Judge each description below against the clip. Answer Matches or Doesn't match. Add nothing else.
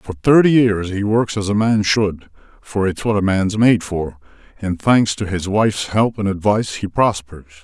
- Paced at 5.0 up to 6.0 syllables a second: Doesn't match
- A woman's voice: Doesn't match